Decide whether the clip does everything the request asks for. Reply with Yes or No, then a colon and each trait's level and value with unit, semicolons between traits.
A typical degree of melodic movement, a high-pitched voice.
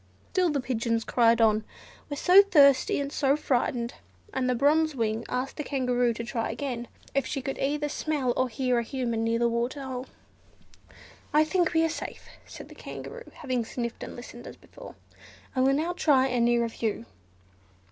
Yes: average, 3.6 semitones; very high, 260 Hz